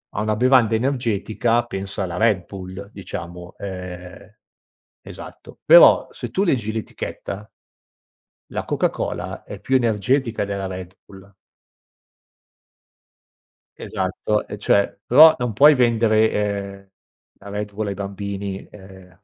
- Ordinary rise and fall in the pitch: Yes, average, 3.0 semitones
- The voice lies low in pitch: Yes, low, 105 Hz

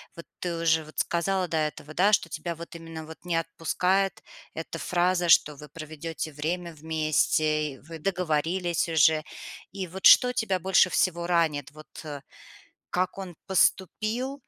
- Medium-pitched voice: Yes, medium, 165 Hz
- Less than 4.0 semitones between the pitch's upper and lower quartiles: Yes, average, 2.8 semitones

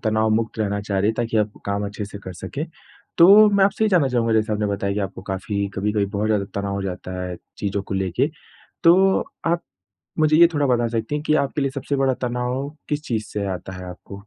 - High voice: No, low, 110 Hz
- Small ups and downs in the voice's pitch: No, wide, 5.6 semitones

